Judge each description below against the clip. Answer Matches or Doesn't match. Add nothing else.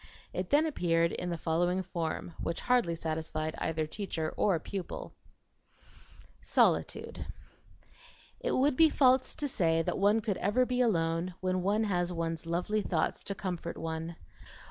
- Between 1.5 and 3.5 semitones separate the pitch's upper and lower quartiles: Doesn't match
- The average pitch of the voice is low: Doesn't match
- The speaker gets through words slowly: Doesn't match